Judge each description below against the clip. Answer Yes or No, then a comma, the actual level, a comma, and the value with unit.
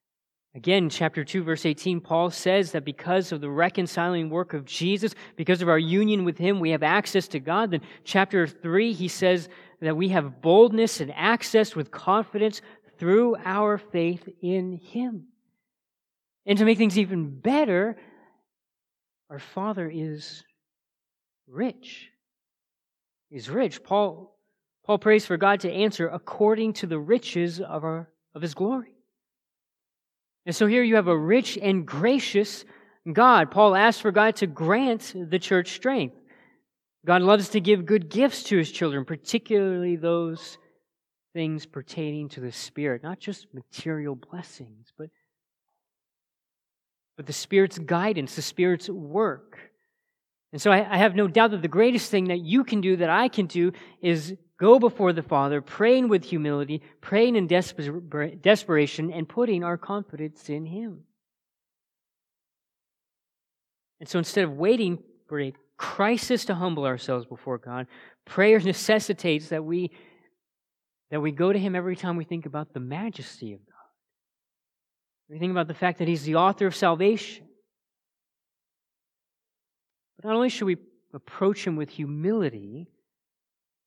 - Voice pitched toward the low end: No, medium, 180 Hz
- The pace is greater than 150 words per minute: No, average, 145 wpm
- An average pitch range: Yes, average, 4.6 semitones